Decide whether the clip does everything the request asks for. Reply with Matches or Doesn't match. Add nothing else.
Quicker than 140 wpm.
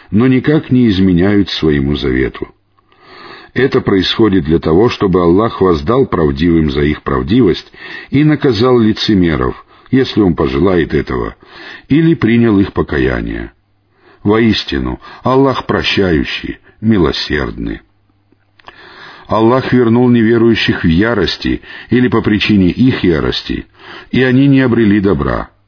Doesn't match